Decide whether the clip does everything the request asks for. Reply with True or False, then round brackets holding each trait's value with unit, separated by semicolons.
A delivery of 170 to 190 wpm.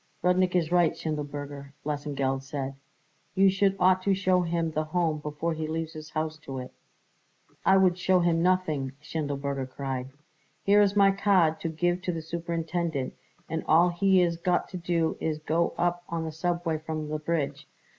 True (180 wpm)